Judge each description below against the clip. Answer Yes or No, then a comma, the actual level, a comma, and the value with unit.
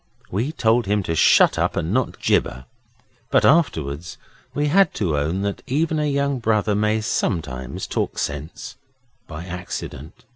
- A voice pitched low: Yes, low, 105 Hz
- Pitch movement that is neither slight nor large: No, wide, 8.4 semitones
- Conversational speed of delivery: Yes, average, 150 wpm